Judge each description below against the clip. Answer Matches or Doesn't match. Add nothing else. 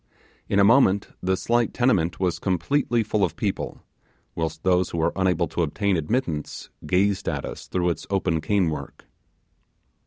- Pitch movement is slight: Doesn't match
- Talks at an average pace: Matches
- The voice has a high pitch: Doesn't match